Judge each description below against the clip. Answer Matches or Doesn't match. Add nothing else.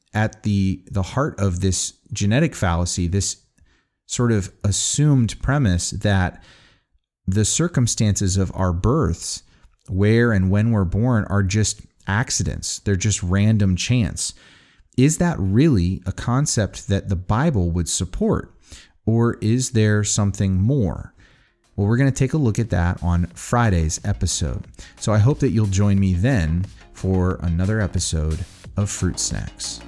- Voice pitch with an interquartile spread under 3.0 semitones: Doesn't match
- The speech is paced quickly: Doesn't match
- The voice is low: Matches